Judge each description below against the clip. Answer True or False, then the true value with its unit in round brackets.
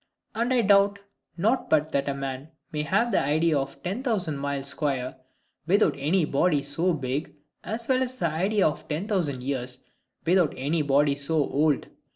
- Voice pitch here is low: False (155 Hz)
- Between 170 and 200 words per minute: True (180 wpm)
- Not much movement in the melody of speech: False (5.5 semitones)